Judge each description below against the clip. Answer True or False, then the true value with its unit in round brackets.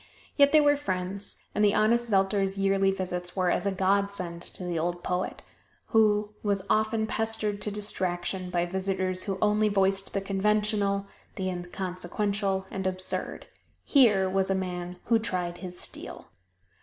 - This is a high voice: True (195 Hz)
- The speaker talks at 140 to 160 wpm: True (155 wpm)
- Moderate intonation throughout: False (2.2 semitones)